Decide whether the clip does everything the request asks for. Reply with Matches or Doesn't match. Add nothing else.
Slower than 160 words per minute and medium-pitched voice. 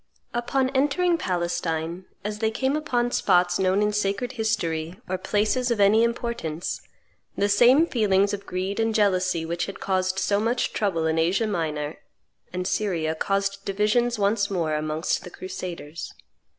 Doesn't match